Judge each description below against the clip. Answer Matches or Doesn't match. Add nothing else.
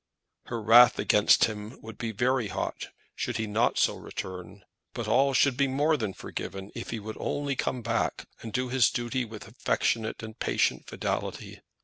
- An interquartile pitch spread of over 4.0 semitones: Doesn't match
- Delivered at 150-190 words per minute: Matches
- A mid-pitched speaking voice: Doesn't match